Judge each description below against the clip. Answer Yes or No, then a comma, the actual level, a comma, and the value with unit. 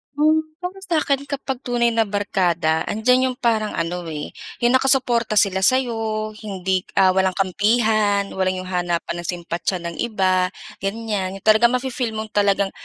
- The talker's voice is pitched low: No, high, 210 Hz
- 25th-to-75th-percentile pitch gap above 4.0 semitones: Yes, average, 4.4 semitones